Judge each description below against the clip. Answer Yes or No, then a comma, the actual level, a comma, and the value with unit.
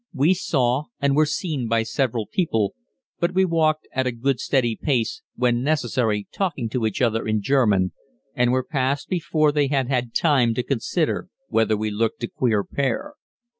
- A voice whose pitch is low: Yes, low, 130 Hz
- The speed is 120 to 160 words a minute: No, average, 175 wpm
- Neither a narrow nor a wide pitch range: Yes, average, 4.6 semitones